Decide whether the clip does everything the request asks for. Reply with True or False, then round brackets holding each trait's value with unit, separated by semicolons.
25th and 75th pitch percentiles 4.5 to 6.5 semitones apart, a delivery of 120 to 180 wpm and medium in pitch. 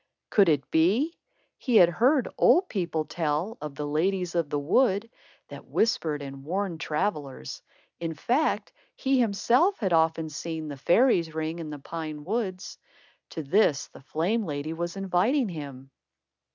True (5.6 semitones; 150 wpm; 170 Hz)